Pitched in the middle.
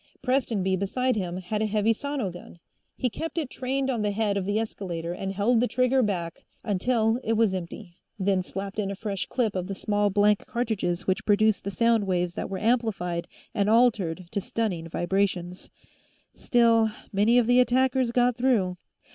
No: high, 210 Hz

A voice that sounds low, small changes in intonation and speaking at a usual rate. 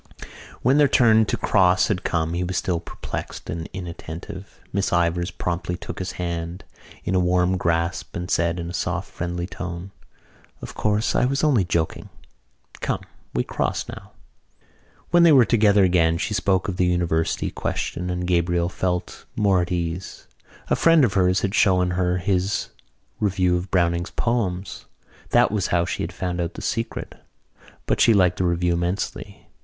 Yes: very low, 90 Hz; narrow, 2.1 semitones; average, 170 wpm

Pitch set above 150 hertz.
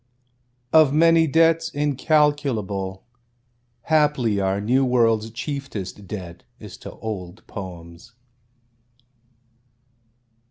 No: low, 115 Hz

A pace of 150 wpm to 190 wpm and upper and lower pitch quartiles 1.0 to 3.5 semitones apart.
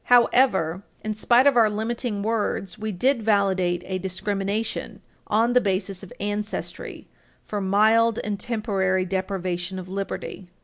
No: slow, 135 wpm; average, 2.9 semitones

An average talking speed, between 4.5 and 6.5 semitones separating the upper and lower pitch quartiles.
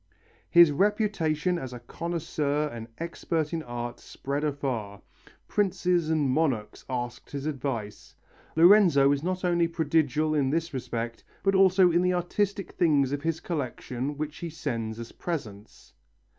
Yes: average, 145 wpm; average, 4.8 semitones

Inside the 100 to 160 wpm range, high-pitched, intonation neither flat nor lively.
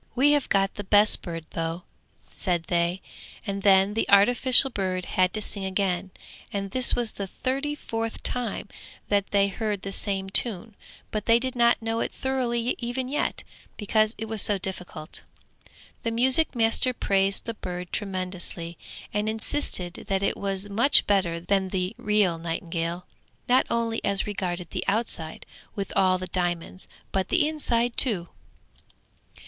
Yes: average, 155 wpm; high, 200 Hz; average, 4.0 semitones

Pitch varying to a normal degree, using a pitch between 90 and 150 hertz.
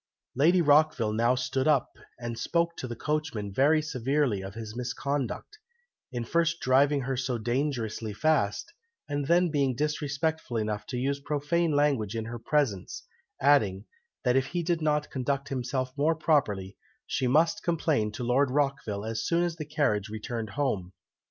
Yes: average, 4.7 semitones; low, 135 Hz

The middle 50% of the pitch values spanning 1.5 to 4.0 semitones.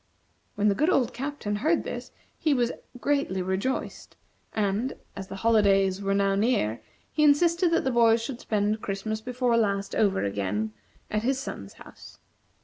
No: average, 4.7 semitones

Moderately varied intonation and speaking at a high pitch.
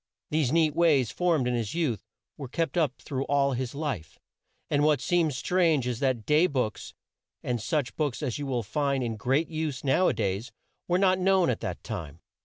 No: average, 4.7 semitones; medium, 140 Hz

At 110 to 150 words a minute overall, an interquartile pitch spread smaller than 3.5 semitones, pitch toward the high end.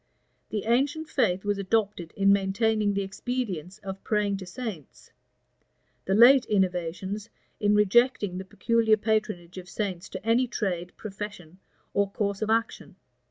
Yes: average, 140 wpm; average, 2.8 semitones; high, 205 Hz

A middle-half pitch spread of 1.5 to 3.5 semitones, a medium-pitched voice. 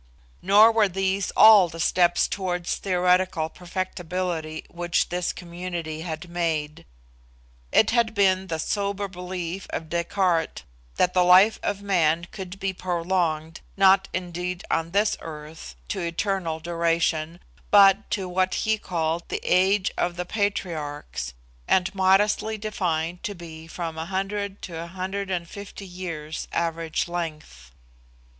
Yes: narrow, 2.6 semitones; medium, 180 Hz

